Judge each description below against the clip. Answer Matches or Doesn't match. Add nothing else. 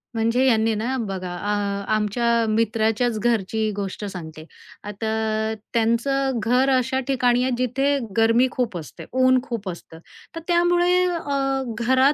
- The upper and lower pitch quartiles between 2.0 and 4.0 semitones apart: Matches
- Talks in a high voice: Matches